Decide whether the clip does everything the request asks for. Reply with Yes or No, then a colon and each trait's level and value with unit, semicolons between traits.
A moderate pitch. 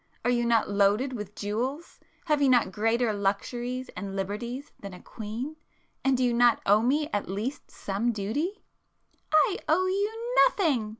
No: high, 240 Hz